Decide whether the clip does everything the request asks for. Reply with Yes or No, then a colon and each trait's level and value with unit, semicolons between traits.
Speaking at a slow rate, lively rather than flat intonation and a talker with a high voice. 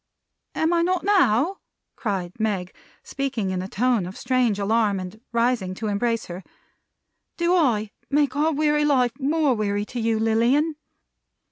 No: average, 150 wpm; wide, 6.1 semitones; high, 235 Hz